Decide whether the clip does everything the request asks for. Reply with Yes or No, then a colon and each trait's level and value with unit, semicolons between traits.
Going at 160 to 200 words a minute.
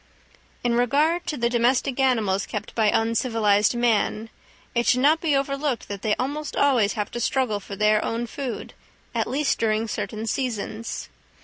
Yes: average, 165 wpm